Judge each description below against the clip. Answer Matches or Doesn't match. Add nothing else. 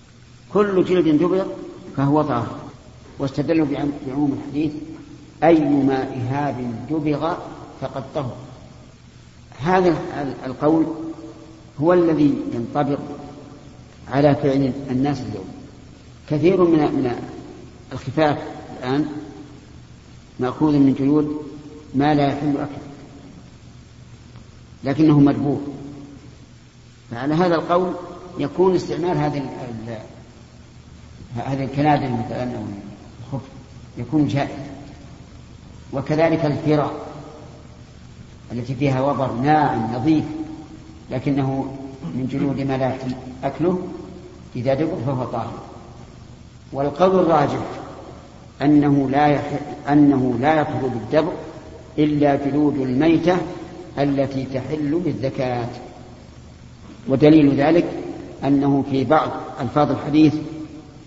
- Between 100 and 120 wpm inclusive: Doesn't match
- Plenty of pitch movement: Doesn't match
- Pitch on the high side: Doesn't match